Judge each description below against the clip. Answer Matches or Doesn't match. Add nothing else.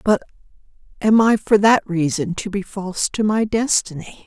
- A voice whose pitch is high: Matches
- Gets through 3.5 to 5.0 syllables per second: Matches